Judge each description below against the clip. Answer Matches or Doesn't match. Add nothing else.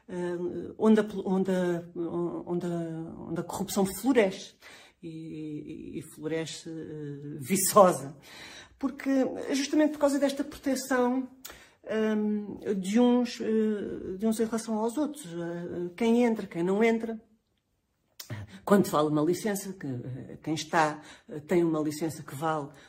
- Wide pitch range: Matches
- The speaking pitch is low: Doesn't match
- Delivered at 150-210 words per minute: Doesn't match